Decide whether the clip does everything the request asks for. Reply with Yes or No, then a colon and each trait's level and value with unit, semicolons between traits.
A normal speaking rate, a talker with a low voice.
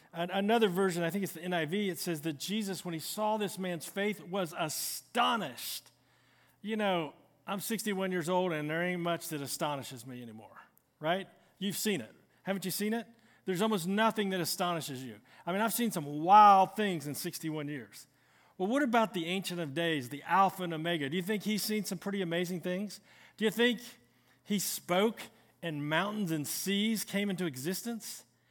No: average, 185 wpm; medium, 185 Hz